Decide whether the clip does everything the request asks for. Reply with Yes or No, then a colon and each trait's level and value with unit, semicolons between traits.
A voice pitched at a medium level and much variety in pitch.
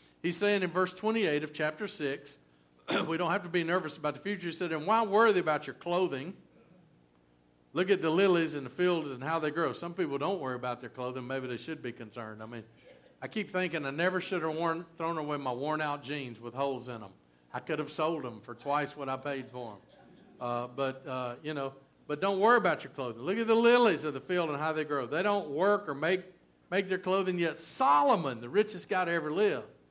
Yes: medium, 155 Hz; wide, 5.9 semitones